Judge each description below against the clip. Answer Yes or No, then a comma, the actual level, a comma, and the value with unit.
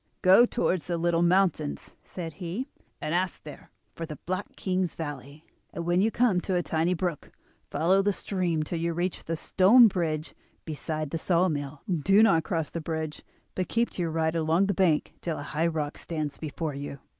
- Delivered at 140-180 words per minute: No, average, 195 wpm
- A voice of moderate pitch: Yes, medium, 170 Hz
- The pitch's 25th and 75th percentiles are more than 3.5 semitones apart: No, average, 2.9 semitones